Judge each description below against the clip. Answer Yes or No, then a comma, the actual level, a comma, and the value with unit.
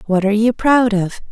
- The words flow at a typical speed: No, fast, 230 wpm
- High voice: Yes, high, 215 Hz